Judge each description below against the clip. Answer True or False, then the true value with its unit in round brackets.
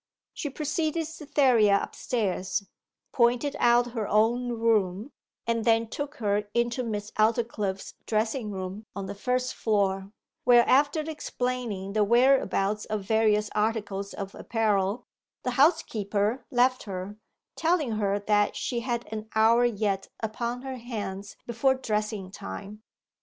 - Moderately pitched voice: False (225 Hz)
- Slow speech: True (130 wpm)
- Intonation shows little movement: False (3.3 semitones)